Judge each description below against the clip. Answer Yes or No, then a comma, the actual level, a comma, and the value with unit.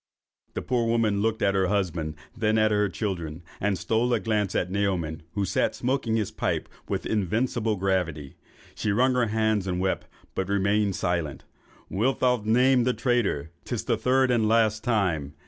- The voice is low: Yes, low, 105 Hz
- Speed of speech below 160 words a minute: No, average, 180 wpm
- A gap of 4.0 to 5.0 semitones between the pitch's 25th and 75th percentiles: No, average, 3.5 semitones